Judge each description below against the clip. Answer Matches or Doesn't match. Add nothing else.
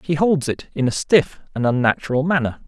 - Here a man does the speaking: Matches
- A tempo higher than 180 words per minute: Matches